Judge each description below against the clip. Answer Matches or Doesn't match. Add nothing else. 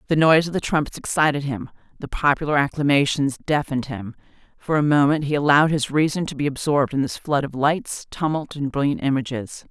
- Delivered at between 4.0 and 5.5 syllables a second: Doesn't match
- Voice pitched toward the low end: Doesn't match